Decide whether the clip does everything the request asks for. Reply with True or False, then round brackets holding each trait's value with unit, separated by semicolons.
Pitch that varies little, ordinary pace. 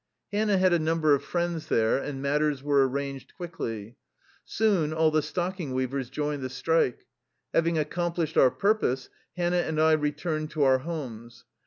False (4.0 semitones; 165 wpm)